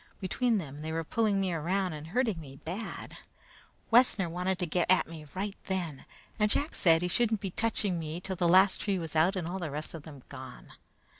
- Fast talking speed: Yes, fast, 215 wpm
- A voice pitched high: No, medium, 180 Hz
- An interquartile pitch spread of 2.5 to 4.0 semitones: Yes, average, 3.6 semitones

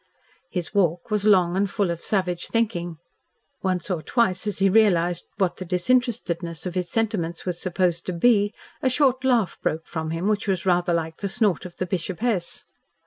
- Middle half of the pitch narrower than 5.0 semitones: Yes, average, 3.4 semitones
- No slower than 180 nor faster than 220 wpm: Yes, average, 185 wpm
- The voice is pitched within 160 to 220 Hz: Yes, medium, 185 Hz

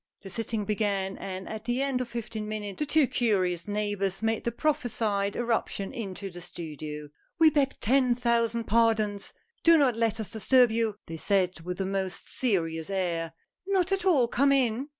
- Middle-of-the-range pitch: No, high, 220 Hz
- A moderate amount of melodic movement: Yes, average, 4.0 semitones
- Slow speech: No, average, 180 wpm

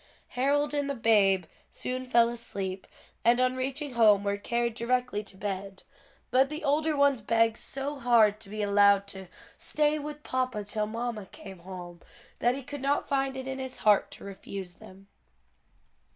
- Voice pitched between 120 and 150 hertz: No, high, 235 Hz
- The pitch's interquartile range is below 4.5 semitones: No, average, 4.8 semitones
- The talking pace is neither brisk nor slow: Yes, average, 170 wpm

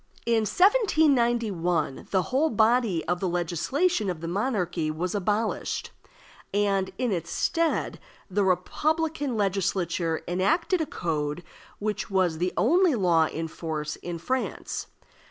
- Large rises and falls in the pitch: Yes, wide, 6.5 semitones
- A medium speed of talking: No, slow, 125 wpm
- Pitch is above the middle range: Yes, high, 195 Hz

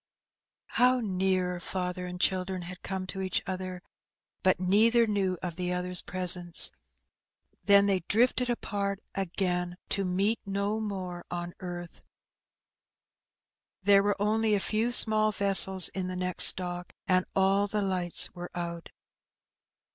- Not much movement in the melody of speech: Yes, narrow, 2.0 semitones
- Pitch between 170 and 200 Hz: Yes, high, 190 Hz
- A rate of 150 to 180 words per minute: No, slow, 135 wpm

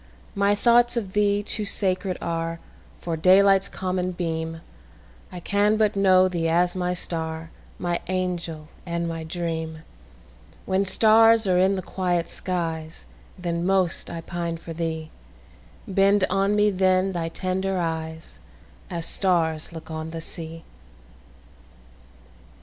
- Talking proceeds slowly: Yes, slow, 115 wpm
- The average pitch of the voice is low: No, medium, 175 Hz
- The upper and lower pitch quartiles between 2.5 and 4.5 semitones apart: Yes, average, 2.8 semitones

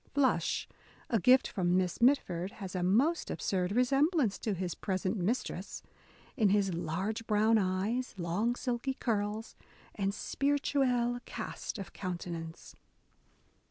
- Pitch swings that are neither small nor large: Yes, average, 4.9 semitones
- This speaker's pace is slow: Yes, slow, 130 wpm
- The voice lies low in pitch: No, high, 210 Hz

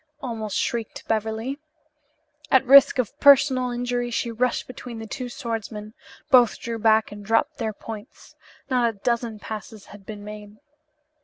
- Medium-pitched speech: No, high, 230 Hz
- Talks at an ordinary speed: Yes, average, 150 wpm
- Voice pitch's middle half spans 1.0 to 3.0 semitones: Yes, narrow, 2.6 semitones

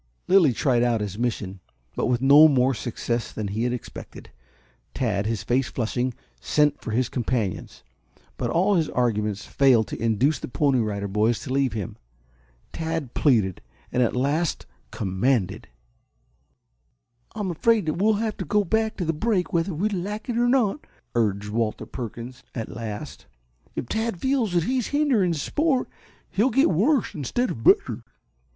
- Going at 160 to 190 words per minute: Yes, average, 165 wpm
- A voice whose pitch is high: No, low, 135 Hz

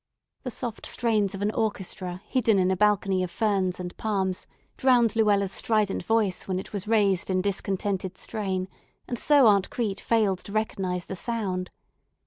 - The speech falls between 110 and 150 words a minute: No, average, 165 wpm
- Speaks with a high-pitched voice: Yes, high, 200 Hz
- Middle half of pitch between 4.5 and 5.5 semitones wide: No, average, 2.8 semitones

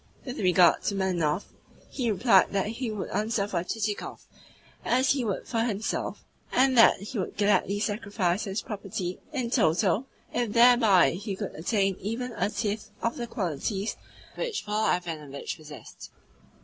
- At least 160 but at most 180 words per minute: No, average, 150 wpm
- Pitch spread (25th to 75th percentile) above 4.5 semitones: No, average, 3.7 semitones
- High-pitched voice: Yes, high, 205 Hz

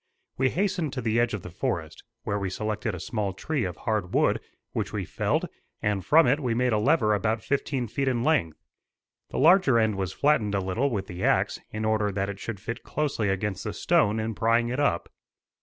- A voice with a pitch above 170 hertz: No, low, 110 Hz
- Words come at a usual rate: No, fast, 215 wpm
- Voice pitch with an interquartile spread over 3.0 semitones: Yes, average, 4.6 semitones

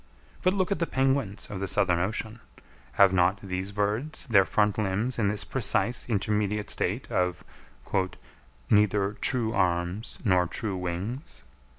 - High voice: No, low, 105 Hz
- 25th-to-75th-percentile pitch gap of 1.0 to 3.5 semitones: Yes, average, 3.1 semitones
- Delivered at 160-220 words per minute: No, average, 145 wpm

